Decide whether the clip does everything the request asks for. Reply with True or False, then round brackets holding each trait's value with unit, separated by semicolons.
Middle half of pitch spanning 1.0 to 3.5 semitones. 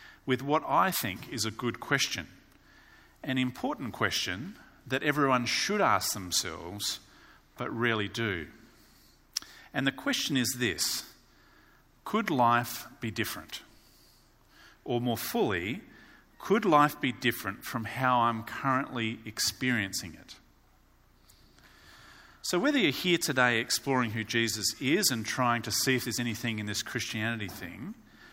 True (2.6 semitones)